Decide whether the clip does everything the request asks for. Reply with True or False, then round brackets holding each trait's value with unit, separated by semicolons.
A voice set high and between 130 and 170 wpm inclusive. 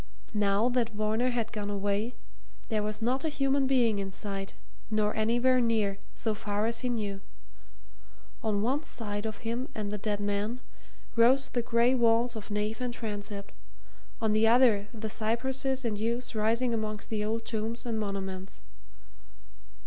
True (220 Hz; 160 wpm)